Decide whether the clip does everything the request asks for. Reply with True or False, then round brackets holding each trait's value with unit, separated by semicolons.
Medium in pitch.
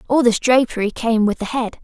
False (235 Hz)